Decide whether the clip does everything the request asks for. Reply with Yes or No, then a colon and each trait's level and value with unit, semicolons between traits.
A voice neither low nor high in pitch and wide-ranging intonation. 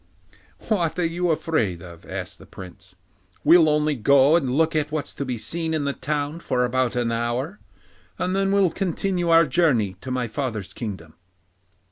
Yes: medium, 145 Hz; wide, 5.7 semitones